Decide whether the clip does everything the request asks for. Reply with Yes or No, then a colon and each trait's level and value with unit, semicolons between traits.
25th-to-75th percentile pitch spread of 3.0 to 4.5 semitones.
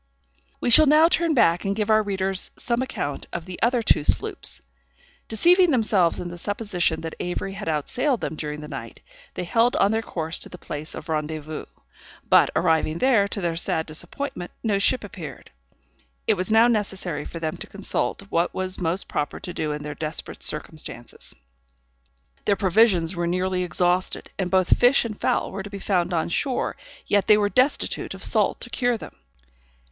No: average, 5.2 semitones